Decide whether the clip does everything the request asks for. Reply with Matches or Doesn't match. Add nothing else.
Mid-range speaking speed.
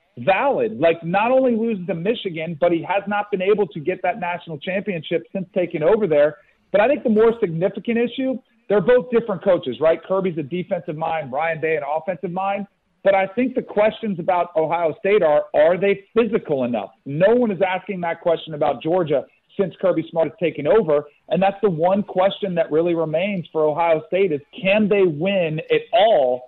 Matches